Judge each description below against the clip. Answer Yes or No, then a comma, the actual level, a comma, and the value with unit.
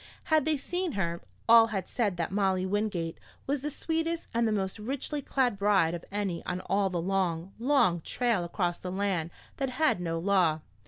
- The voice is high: Yes, high, 200 Hz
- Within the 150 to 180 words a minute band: No, average, 190 wpm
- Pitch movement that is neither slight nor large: No, wide, 6.0 semitones